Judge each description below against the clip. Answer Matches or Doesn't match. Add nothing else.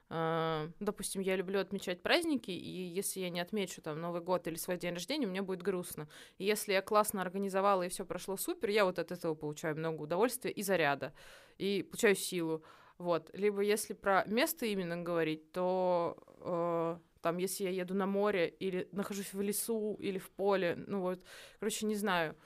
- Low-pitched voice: Doesn't match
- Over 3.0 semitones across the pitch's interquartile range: Doesn't match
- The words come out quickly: Matches